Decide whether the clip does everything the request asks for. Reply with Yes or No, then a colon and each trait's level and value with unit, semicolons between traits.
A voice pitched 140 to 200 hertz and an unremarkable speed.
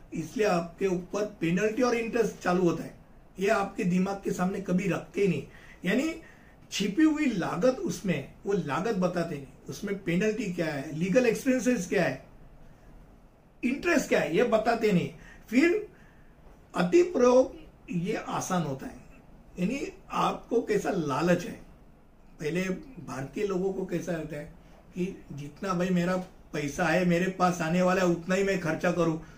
Yes: medium, 185 Hz; average, 155 wpm